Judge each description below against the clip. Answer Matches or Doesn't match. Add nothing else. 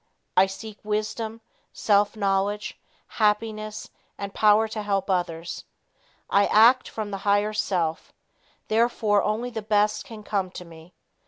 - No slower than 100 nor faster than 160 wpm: Matches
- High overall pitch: Matches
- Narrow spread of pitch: Matches